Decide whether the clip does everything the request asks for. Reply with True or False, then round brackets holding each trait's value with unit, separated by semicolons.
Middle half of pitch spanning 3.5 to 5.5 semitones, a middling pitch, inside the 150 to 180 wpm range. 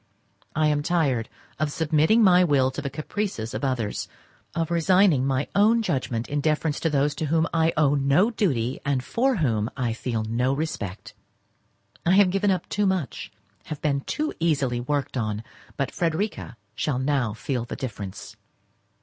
True (4.8 semitones; 145 Hz; 165 wpm)